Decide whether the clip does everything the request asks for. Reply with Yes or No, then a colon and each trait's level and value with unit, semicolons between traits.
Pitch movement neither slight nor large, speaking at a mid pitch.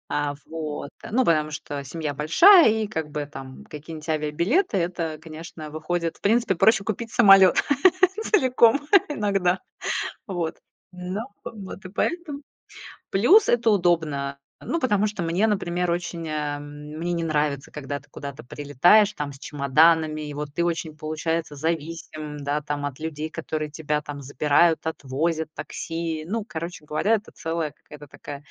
Yes: average, 4.2 semitones; medium, 160 Hz